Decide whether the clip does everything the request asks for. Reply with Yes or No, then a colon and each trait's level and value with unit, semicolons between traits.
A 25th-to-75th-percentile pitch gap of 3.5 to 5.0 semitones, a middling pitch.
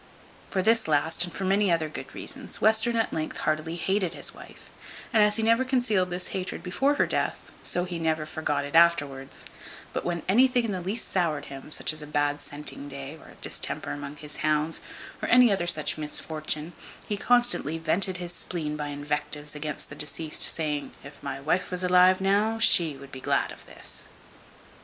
Yes: average, 4.4 semitones; medium, 165 Hz